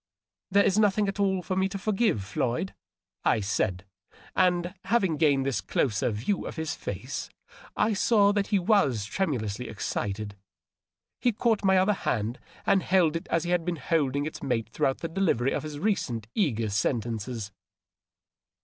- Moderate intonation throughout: No, wide, 8.8 semitones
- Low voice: No, medium, 160 Hz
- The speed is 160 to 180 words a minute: Yes, average, 170 wpm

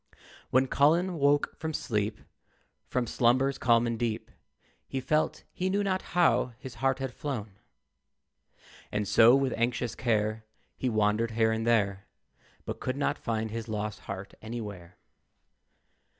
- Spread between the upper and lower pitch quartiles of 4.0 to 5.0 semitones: No, average, 3.6 semitones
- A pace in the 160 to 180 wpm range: No, average, 140 wpm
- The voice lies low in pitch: Yes, low, 120 Hz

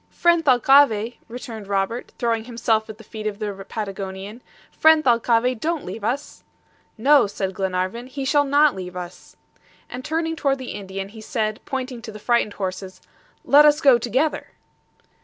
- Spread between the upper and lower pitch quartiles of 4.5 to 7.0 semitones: Yes, average, 5.0 semitones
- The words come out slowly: No, average, 160 wpm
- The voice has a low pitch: No, high, 230 Hz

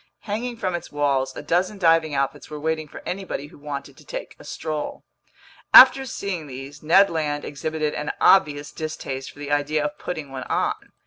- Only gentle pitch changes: No, average, 3.2 semitones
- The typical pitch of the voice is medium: Yes, medium, 150 Hz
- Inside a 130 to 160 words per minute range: No, average, 185 wpm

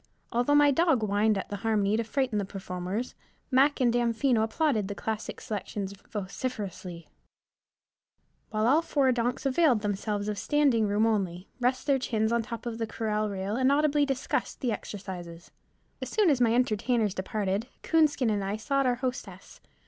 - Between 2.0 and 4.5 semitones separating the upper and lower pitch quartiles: Yes, average, 4.1 semitones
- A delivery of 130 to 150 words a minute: No, average, 165 wpm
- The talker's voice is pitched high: Yes, high, 225 Hz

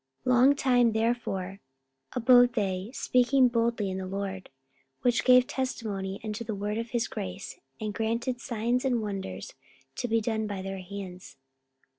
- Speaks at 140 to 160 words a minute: Yes, average, 155 wpm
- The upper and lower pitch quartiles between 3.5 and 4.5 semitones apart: Yes, average, 3.8 semitones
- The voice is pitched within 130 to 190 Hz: No, high, 225 Hz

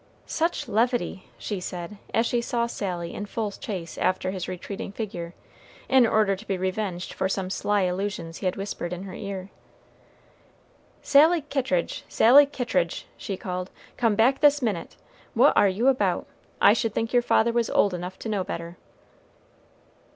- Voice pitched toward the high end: Yes, high, 200 Hz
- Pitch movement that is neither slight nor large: Yes, average, 4.3 semitones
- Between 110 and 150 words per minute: No, average, 165 wpm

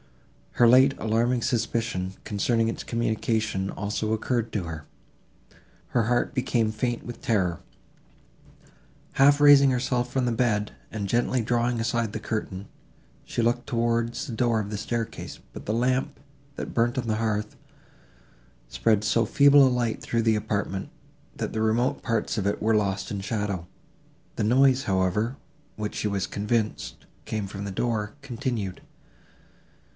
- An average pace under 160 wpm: Yes, average, 150 wpm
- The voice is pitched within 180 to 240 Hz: No, low, 115 Hz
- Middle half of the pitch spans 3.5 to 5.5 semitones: No, narrow, 2.6 semitones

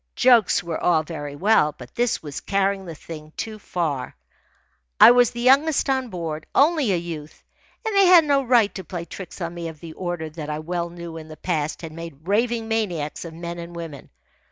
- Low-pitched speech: No, medium, 175 Hz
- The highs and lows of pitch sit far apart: Yes, wide, 5.9 semitones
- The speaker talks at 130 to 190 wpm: No, fast, 205 wpm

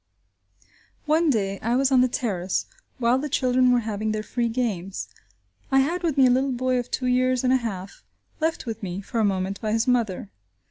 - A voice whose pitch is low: No, high, 245 Hz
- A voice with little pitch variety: No, average, 3.3 semitones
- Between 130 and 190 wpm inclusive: No, fast, 205 wpm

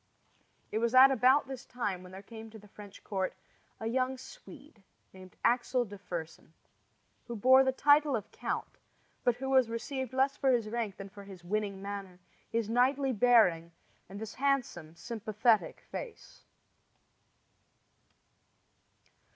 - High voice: Yes, high, 230 Hz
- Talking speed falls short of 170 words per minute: Yes, average, 145 wpm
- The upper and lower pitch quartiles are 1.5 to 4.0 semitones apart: No, average, 4.6 semitones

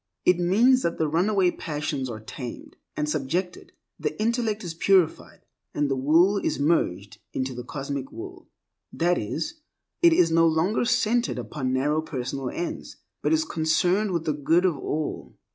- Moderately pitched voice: Yes, medium, 160 Hz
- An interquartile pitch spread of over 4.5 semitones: Yes, average, 5.3 semitones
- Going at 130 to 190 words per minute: Yes, average, 160 wpm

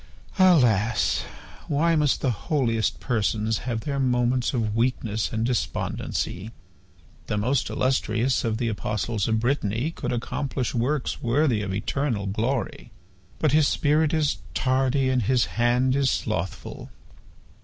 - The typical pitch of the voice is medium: No, low, 125 Hz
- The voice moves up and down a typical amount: Yes, average, 3.7 semitones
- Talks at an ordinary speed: No, slow, 130 wpm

